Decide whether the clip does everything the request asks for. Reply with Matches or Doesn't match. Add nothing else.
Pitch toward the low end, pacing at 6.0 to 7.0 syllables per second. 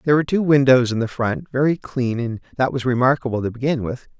Matches